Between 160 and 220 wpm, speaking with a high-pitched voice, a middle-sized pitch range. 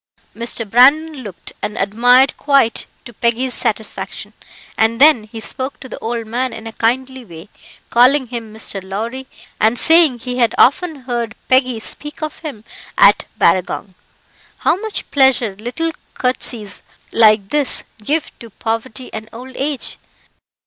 No: average, 145 wpm; high, 245 Hz; average, 3.1 semitones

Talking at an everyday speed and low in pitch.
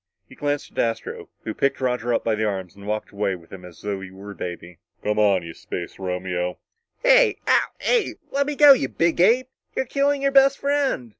No: fast, 225 wpm; low, 110 Hz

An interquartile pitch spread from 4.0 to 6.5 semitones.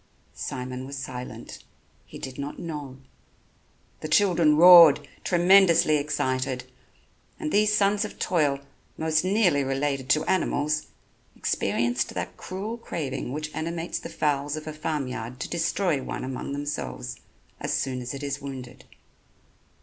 Yes: average, 4.3 semitones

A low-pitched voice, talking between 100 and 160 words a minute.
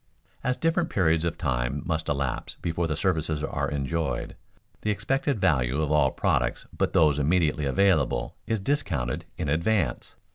Yes: very low, 80 Hz; average, 145 wpm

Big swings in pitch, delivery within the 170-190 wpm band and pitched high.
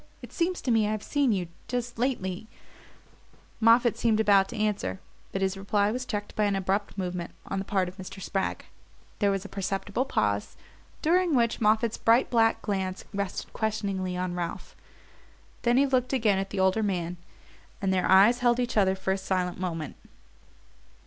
No: average, 3.5 semitones; average, 180 wpm; high, 200 Hz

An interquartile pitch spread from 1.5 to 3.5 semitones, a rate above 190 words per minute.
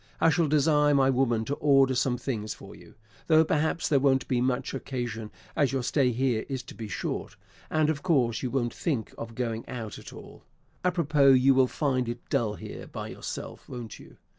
Yes: average, 3.2 semitones; average, 200 wpm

